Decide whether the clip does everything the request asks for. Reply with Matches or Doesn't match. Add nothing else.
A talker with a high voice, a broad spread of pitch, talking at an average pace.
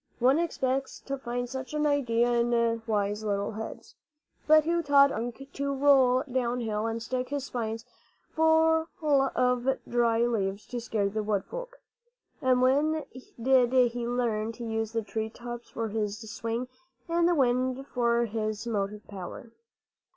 Doesn't match